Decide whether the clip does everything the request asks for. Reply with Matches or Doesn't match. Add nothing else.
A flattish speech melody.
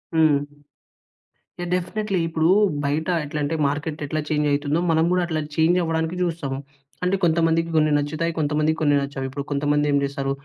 Matches